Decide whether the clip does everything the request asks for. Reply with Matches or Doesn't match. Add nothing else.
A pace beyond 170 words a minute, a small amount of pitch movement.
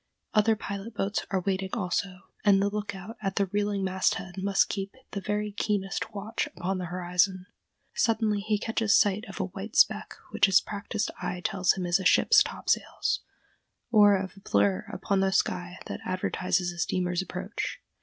Matches